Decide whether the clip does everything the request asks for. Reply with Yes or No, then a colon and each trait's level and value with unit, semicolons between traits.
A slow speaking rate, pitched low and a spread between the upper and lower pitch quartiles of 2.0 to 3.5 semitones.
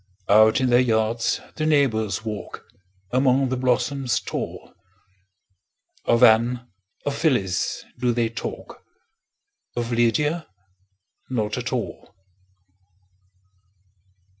Yes: slow, 95 wpm; low, 120 Hz; narrow, 2.6 semitones